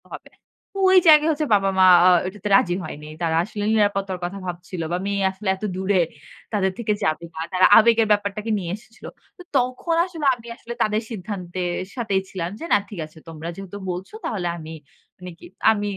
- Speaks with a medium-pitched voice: No, high, 195 Hz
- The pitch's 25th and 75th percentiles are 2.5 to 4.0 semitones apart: Yes, average, 3.3 semitones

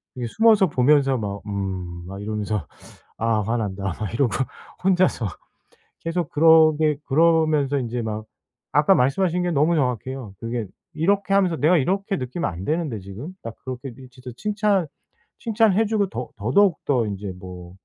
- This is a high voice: No, low, 135 Hz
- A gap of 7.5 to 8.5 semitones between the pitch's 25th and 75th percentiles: Yes, wide, 7.9 semitones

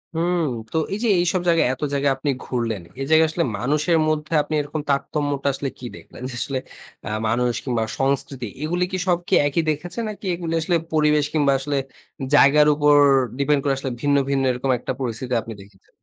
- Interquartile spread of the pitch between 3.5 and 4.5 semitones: No, average, 2.9 semitones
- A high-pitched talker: No, medium, 145 Hz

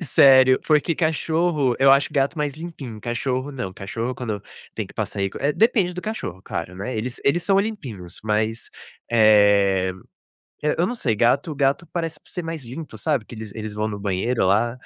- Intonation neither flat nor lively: No, wide, 6.5 semitones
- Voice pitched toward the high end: No, low, 130 Hz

